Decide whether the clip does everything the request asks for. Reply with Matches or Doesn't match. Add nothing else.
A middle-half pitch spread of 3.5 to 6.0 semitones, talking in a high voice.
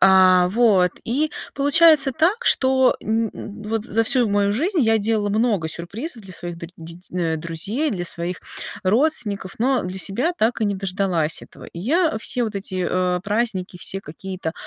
Matches